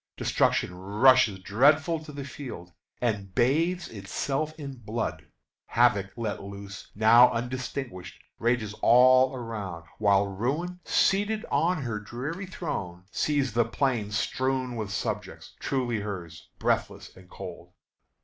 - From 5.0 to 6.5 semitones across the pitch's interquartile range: Yes, wide, 5.4 semitones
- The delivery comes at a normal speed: No, slow, 120 wpm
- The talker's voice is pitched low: Yes, low, 120 Hz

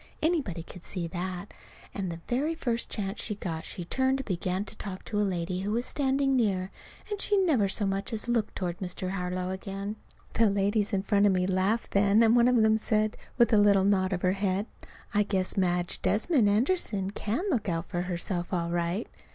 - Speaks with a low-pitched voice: No, high, 200 Hz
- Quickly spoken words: Yes, fast, 210 wpm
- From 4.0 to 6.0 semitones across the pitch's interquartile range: No, average, 3.5 semitones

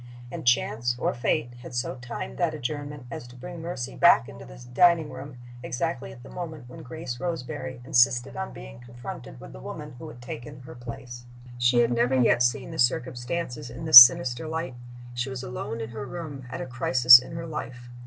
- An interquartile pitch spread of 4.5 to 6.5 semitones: No, average, 3.2 semitones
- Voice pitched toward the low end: Yes, low, 125 Hz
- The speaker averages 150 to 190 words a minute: No, average, 200 wpm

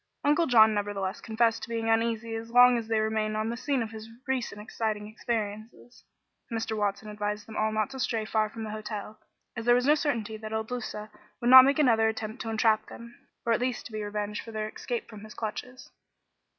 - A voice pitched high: Yes, high, 220 Hz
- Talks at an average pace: No, fast, 215 wpm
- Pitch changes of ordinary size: No, narrow, 1.7 semitones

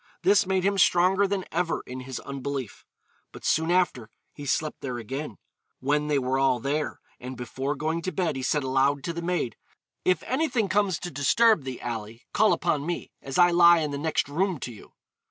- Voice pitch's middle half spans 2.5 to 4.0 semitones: No, average, 5.2 semitones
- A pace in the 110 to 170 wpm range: No, average, 200 wpm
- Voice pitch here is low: No, medium, 150 Hz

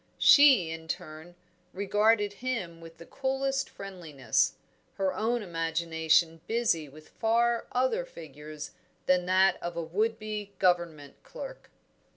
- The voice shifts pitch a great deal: Yes, wide, 5.8 semitones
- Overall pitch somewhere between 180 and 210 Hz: Yes, medium, 185 Hz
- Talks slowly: Yes, slow, 125 wpm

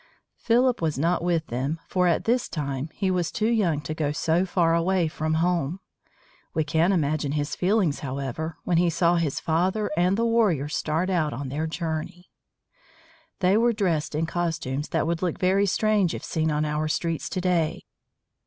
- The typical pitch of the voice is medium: Yes, medium, 165 Hz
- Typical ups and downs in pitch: Yes, average, 3.1 semitones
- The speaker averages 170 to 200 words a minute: Yes, average, 180 wpm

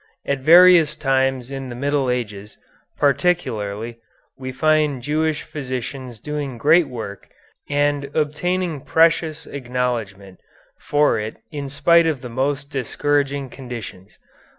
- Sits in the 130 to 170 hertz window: Yes, medium, 140 Hz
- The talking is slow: Yes, slow, 120 wpm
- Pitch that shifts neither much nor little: Yes, average, 3.3 semitones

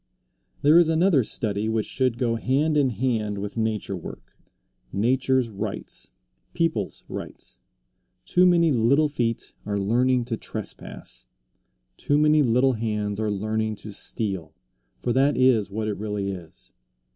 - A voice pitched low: Yes, low, 115 Hz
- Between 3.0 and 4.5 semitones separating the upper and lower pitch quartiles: Yes, average, 4.2 semitones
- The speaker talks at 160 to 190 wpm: No, average, 140 wpm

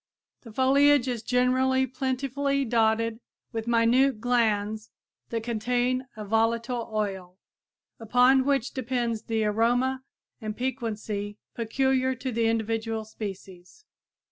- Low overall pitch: No, high, 235 Hz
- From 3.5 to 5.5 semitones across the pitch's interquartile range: No, average, 2.8 semitones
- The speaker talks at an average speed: No, slow, 110 wpm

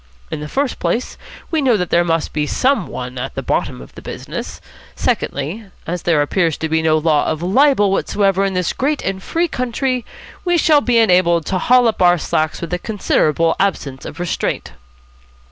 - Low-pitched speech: No, medium, 180 Hz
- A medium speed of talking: Yes, average, 195 wpm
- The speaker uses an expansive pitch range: Yes, wide, 6.8 semitones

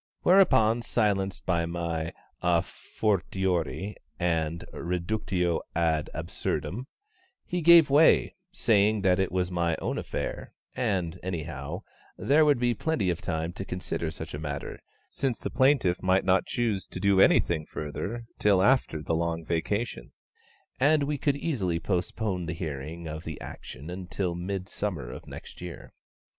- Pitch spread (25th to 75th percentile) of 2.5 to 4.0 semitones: No, average, 4.7 semitones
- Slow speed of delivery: No, average, 145 wpm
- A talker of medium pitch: No, very low, 90 Hz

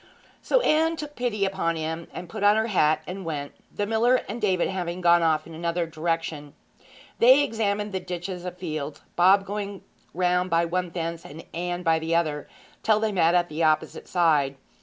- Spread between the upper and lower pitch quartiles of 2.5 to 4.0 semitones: Yes, average, 3.5 semitones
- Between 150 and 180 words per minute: No, average, 190 wpm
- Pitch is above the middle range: No, medium, 175 Hz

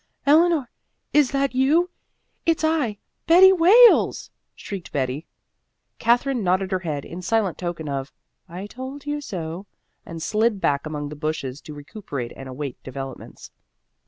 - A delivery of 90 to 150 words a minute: Yes, average, 140 wpm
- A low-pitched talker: No, high, 195 Hz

